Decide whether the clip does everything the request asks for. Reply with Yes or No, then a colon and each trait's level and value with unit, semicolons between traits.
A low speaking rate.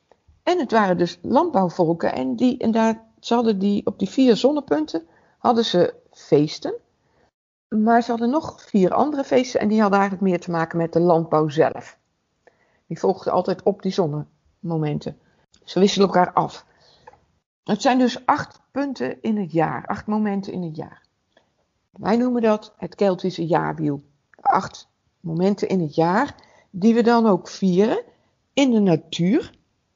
No: average, 155 wpm